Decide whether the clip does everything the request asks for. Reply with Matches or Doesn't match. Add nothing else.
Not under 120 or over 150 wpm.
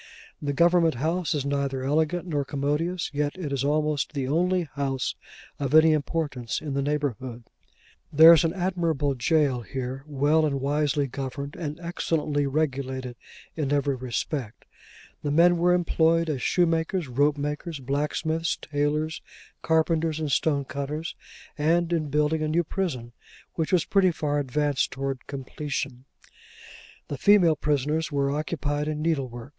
Matches